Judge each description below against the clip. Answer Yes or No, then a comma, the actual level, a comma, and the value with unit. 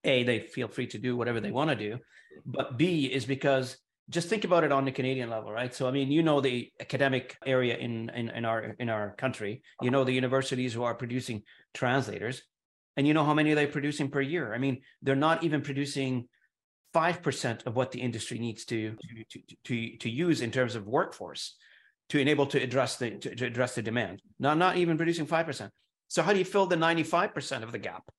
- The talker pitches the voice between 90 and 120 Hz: No, low, 135 Hz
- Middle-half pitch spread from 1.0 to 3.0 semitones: No, average, 4.0 semitones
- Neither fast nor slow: No, fast, 225 wpm